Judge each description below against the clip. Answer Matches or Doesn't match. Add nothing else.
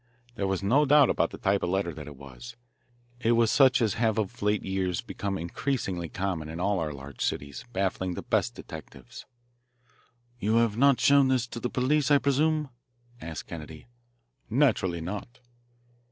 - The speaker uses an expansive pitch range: Matches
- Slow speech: Doesn't match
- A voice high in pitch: Doesn't match